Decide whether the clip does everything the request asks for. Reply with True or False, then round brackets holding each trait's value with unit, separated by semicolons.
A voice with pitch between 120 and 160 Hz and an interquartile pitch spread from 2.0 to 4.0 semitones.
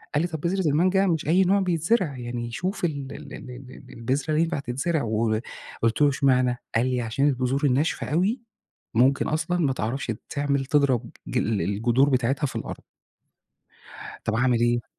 False (135 Hz; 4.7 semitones)